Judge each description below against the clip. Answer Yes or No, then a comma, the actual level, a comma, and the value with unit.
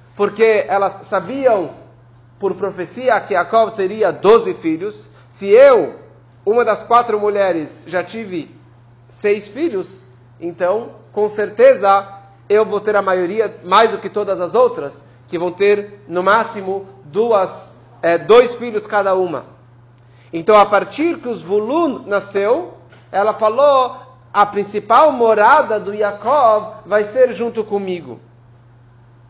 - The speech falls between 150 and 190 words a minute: No, average, 125 wpm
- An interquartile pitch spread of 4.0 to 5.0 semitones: Yes, average, 4.7 semitones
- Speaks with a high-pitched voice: Yes, high, 200 Hz